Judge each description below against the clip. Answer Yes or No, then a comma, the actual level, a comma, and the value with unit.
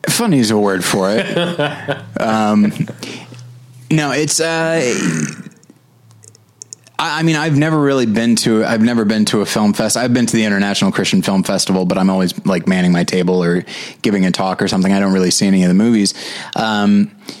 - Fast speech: No, average, 190 wpm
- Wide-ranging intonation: Yes, wide, 7.0 semitones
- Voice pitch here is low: Yes, low, 115 Hz